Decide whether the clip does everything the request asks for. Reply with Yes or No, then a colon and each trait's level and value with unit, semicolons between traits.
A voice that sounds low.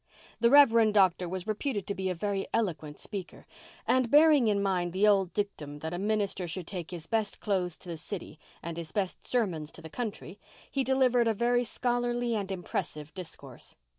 No: high, 200 Hz